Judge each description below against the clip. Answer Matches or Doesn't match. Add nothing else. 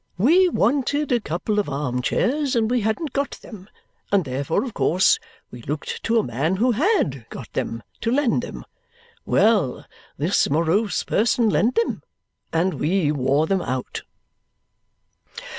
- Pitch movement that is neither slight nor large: Doesn't match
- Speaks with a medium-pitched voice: Doesn't match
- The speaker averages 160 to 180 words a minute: Doesn't match